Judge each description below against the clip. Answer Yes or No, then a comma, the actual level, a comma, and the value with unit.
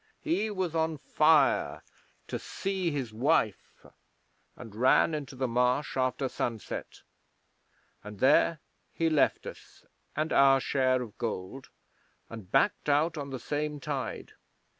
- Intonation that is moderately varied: Yes, average, 3.7 semitones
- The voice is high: No, low, 135 Hz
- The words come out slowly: Yes, slow, 130 wpm